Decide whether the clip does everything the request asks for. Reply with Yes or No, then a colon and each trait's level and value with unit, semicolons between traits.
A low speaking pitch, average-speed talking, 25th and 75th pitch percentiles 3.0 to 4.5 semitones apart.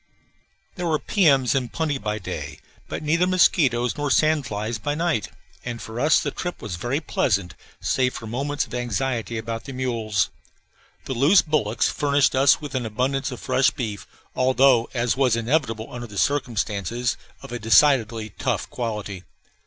Yes: low, 125 Hz; average, 160 wpm; average, 4.1 semitones